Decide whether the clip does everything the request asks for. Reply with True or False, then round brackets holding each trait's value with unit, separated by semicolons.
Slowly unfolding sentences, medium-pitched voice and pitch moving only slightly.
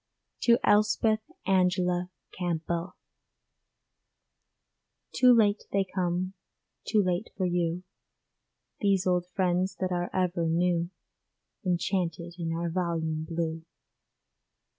True (95 wpm; 180 Hz; 1.8 semitones)